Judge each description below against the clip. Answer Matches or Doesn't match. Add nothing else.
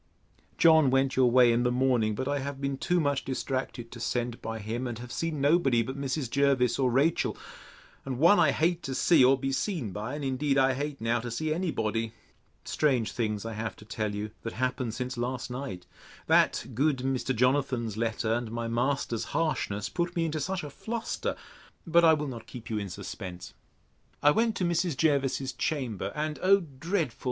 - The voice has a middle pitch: Doesn't match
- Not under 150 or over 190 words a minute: Doesn't match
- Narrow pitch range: Doesn't match